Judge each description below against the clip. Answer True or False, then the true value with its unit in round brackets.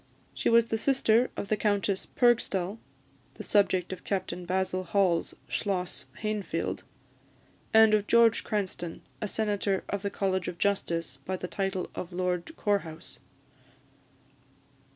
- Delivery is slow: True (130 wpm)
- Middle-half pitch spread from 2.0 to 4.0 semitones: True (2.7 semitones)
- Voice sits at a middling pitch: False (195 Hz)